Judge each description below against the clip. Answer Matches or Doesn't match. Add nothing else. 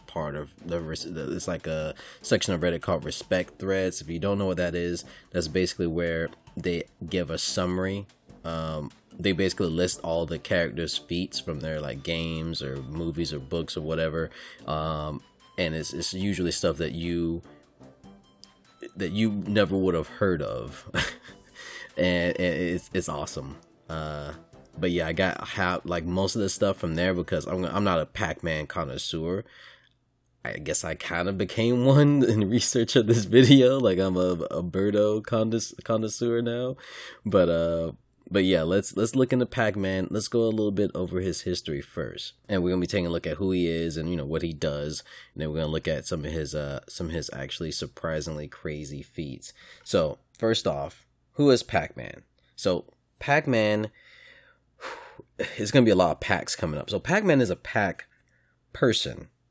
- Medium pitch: Doesn't match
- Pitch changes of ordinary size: Matches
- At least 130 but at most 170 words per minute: Doesn't match